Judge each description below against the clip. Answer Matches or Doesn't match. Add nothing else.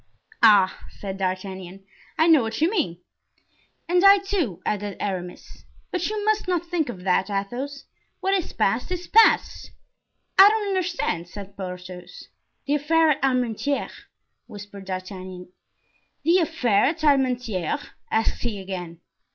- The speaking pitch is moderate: Doesn't match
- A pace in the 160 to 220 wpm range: Doesn't match